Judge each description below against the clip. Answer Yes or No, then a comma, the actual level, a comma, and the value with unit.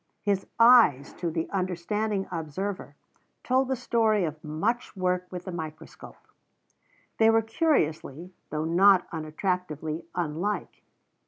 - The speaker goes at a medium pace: No, slow, 115 wpm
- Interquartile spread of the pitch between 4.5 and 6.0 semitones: Yes, average, 4.9 semitones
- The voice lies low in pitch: No, medium, 180 Hz